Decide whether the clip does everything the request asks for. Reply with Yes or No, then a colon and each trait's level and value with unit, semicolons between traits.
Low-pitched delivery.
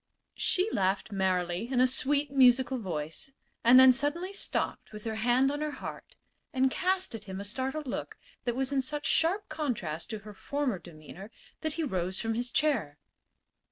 No: very high, 250 Hz